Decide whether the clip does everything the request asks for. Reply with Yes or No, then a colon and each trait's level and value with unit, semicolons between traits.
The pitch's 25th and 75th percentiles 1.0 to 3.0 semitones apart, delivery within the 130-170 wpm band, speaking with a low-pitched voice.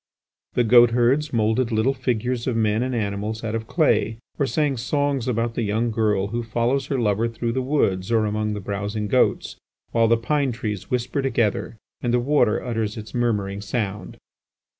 No: average, 2.7 semitones; average, 180 wpm; low, 115 Hz